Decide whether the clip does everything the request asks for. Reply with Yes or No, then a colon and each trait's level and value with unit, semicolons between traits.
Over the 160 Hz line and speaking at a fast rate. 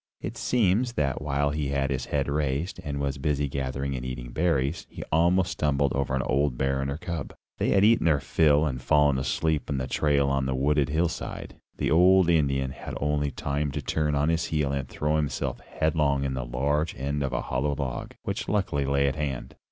No: very low, 70 Hz; fast, 210 wpm